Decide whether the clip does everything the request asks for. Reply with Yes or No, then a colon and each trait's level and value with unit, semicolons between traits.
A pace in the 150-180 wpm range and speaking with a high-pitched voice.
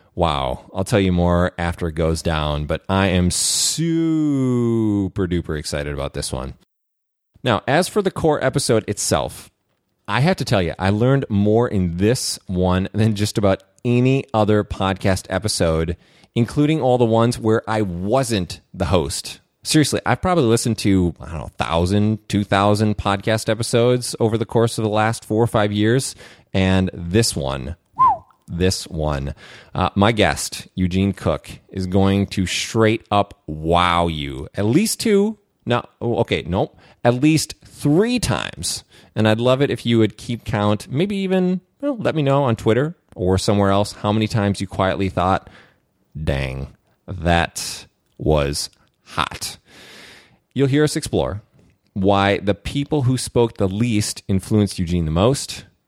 No: average, 160 wpm; low, 105 Hz